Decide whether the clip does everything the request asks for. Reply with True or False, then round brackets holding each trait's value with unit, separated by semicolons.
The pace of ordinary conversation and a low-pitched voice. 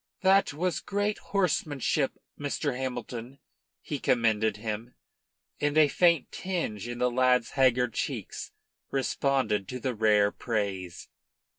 False (120 wpm; 125 Hz)